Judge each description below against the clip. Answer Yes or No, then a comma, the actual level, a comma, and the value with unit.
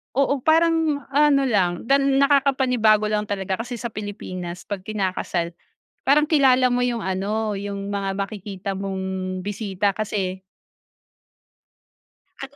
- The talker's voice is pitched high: Yes, high, 210 Hz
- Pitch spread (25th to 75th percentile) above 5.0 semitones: Yes, wide, 5.6 semitones